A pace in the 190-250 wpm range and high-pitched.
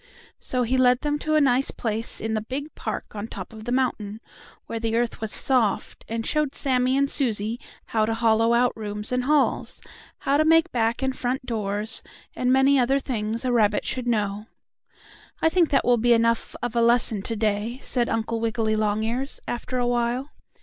Yes: average, 195 wpm; high, 235 Hz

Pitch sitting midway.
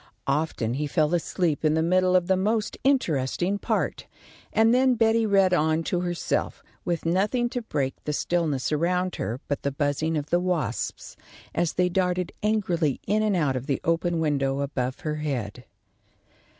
Yes: medium, 170 Hz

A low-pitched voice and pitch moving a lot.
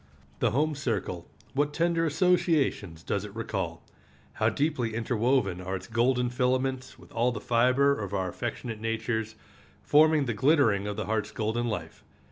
No: low, 120 Hz; average, 4.7 semitones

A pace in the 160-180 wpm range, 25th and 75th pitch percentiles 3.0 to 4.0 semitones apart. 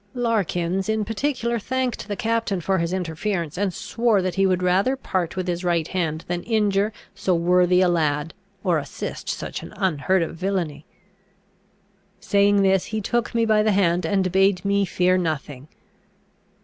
Yes: average, 170 wpm; average, 3.3 semitones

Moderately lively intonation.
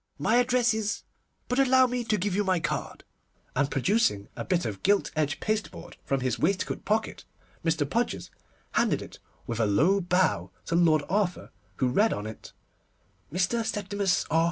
No: wide, 6.2 semitones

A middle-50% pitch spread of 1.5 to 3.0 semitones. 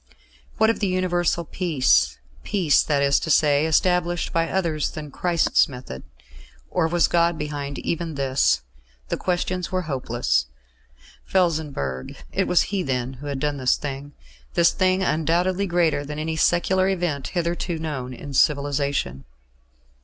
No: average, 3.9 semitones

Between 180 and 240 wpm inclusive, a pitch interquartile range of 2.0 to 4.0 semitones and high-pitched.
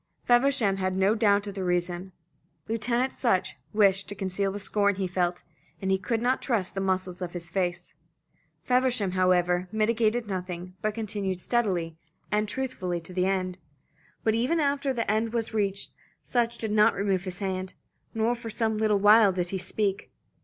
No: average, 170 wpm; average, 3.4 semitones; high, 200 Hz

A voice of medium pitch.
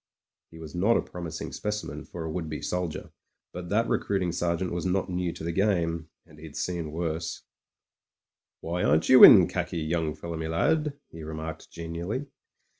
No: very low, 85 Hz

